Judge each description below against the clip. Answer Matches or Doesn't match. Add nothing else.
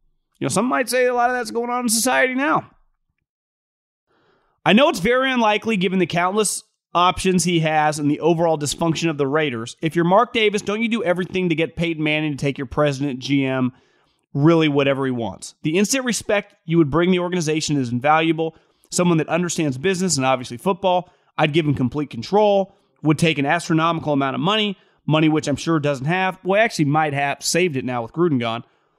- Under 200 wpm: Doesn't match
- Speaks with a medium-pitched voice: Matches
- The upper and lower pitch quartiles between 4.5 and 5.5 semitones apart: Matches